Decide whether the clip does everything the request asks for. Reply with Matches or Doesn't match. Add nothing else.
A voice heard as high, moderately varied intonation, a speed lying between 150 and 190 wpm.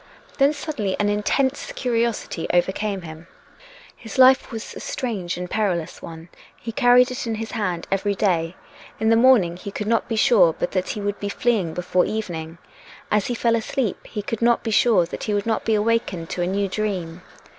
Doesn't match